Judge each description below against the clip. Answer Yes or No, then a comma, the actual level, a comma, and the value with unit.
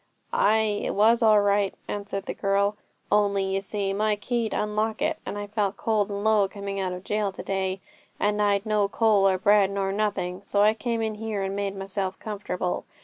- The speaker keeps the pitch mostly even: Yes, narrow, 1.4 semitones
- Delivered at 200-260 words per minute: Yes, fast, 205 wpm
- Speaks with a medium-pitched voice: No, high, 205 Hz